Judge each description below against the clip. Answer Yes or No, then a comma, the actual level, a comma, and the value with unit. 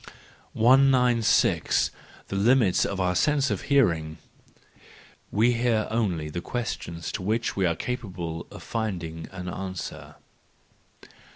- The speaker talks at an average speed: No, slow, 115 wpm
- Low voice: Yes, low, 100 Hz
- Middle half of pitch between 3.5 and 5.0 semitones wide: No, wide, 5.5 semitones